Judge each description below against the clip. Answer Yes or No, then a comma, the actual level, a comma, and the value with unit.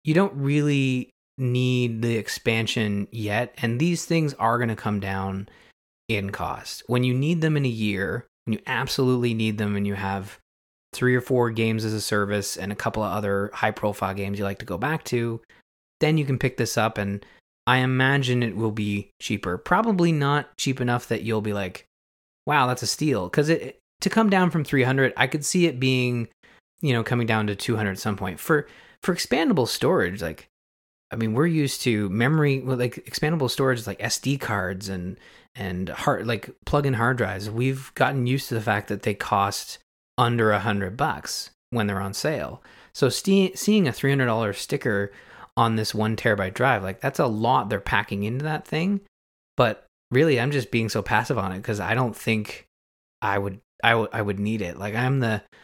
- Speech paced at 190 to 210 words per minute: Yes, average, 200 wpm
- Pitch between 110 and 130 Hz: Yes, low, 115 Hz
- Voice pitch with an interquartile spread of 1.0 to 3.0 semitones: No, average, 4.5 semitones